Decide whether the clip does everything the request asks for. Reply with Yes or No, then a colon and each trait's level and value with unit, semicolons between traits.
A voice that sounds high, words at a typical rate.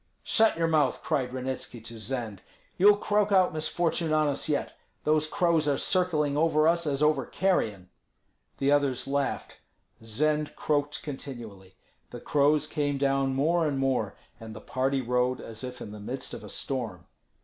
No: medium, 140 Hz; average, 165 wpm